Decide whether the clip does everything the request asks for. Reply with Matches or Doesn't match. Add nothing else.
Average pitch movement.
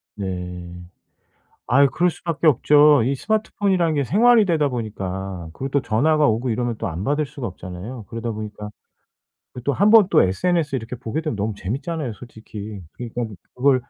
Doesn't match